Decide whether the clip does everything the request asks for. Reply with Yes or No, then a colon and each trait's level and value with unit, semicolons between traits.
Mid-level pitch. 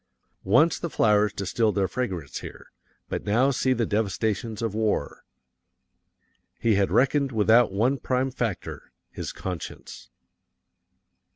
No: low, 110 Hz